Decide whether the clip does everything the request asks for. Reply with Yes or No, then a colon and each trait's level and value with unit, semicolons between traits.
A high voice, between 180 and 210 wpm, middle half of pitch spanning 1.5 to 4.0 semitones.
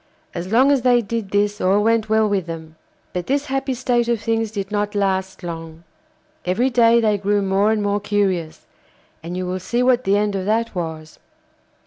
Yes: high, 205 Hz; average, 195 wpm; average, 3.6 semitones